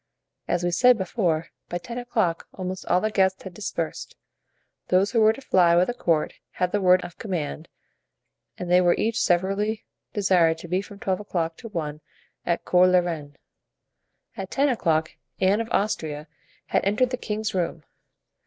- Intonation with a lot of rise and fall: No, average, 3.6 semitones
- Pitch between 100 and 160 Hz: No, medium, 185 Hz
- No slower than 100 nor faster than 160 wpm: No, average, 175 wpm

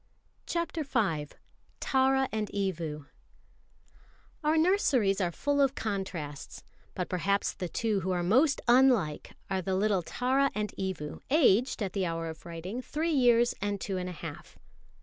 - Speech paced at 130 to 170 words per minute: Yes, average, 160 wpm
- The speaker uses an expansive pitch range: Yes, wide, 6.4 semitones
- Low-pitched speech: No, high, 205 Hz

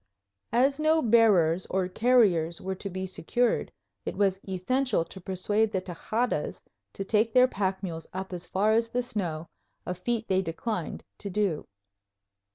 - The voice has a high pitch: Yes, high, 195 Hz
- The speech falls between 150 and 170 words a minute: Yes, average, 160 wpm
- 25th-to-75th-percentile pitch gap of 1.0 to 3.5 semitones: No, average, 4.0 semitones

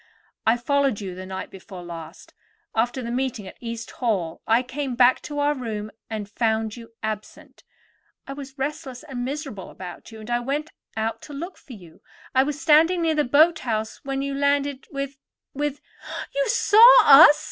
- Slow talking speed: No, average, 180 wpm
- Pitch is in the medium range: No, very high, 260 Hz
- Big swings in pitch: No, average, 4.7 semitones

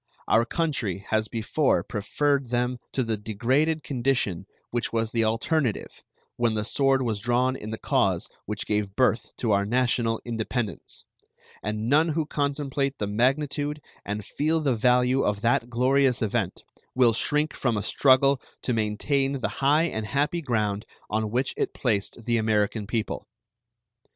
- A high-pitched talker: No, low, 120 Hz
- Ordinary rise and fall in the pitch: Yes, average, 4.0 semitones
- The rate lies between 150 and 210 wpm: Yes, average, 155 wpm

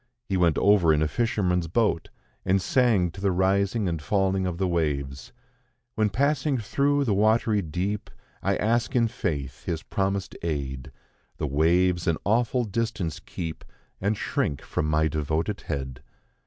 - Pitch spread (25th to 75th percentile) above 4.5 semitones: Yes, average, 5.2 semitones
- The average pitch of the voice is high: No, very low, 95 Hz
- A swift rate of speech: No, average, 155 wpm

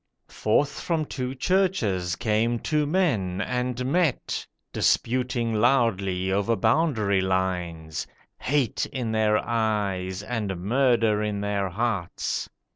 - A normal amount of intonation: Yes, average, 4.6 semitones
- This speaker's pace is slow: Yes, slow, 110 wpm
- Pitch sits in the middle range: No, low, 110 Hz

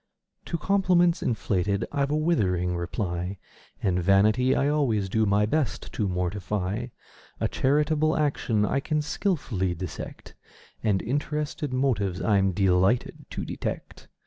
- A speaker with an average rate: No, slow, 125 wpm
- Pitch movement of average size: No, wide, 7.4 semitones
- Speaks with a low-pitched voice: Yes, low, 110 Hz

